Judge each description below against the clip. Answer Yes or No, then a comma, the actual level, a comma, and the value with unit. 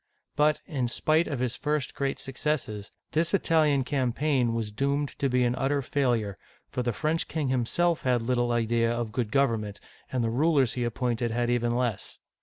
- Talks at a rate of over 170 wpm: Yes, average, 185 wpm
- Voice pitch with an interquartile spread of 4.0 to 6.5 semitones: No, average, 3.5 semitones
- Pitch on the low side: Yes, low, 125 Hz